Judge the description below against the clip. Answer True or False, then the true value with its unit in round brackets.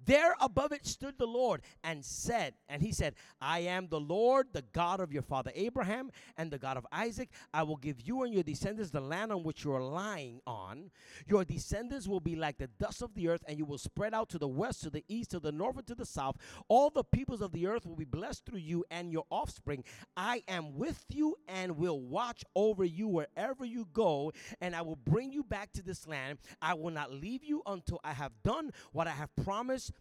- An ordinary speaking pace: False (235 wpm)